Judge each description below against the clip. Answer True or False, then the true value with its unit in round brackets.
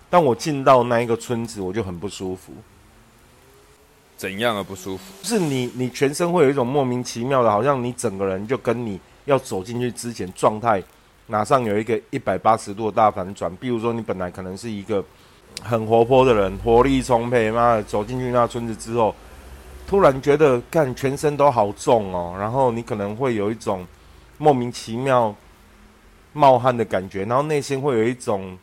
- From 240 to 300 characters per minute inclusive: True (280 characters per minute)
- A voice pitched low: True (115 Hz)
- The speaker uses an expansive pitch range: False (4.2 semitones)